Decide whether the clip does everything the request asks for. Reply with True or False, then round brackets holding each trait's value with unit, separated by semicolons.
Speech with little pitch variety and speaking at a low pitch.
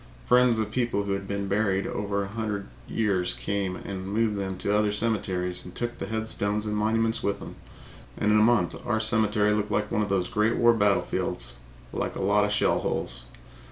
True (1.9 semitones; 105 Hz)